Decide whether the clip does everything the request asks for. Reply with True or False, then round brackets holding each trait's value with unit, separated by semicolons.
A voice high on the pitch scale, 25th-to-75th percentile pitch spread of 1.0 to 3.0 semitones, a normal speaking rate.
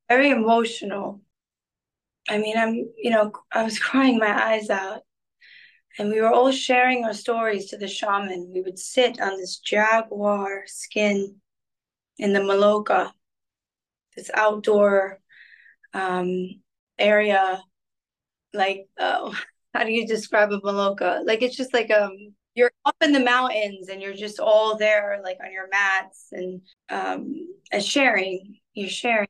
True (210 Hz; 2.7 semitones; 145 wpm)